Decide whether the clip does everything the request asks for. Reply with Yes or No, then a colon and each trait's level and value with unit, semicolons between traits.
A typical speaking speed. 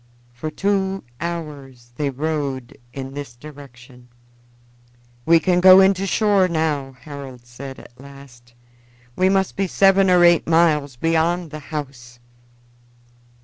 No: slow, 130 wpm